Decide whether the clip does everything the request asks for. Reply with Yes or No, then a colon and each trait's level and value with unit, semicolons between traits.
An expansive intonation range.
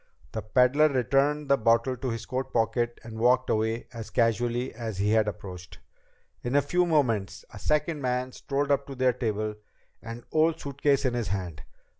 No: average, 3.8 semitones